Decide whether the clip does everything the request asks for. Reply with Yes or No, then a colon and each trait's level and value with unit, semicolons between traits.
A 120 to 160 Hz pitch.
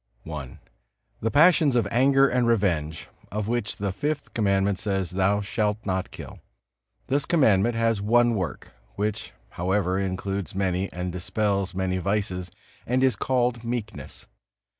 No: low, 100 Hz